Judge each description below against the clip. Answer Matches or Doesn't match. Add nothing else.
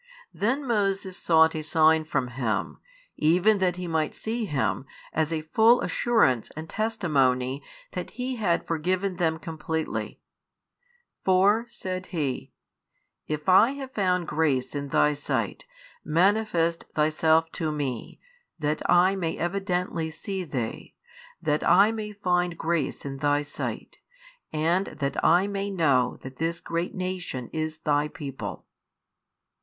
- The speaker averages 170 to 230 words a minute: Doesn't match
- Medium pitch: Matches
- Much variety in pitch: Doesn't match